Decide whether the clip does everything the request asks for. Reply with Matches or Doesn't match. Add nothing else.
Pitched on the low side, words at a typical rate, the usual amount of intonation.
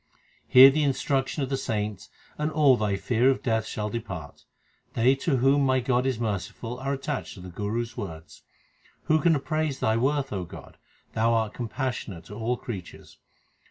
Matches